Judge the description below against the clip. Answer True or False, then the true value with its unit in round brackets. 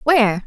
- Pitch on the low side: False (240 Hz)